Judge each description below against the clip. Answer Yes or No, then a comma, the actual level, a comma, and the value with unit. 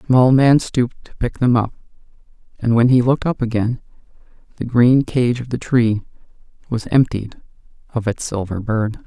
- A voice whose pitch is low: Yes, low, 120 Hz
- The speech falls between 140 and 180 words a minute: Yes, average, 170 wpm